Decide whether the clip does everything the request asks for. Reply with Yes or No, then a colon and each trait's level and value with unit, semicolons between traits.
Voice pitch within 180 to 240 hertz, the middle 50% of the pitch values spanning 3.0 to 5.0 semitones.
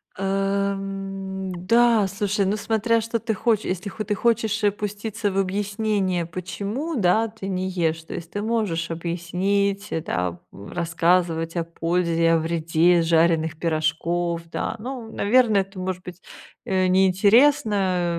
Yes: high, 190 Hz; average, 3.4 semitones